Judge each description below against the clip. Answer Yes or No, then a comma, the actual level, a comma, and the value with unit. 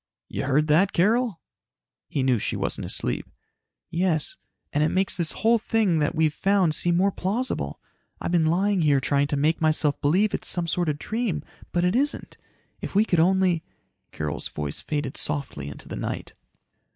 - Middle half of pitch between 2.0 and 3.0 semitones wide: No, average, 4.5 semitones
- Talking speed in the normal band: Yes, average, 180 wpm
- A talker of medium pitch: Yes, medium, 165 Hz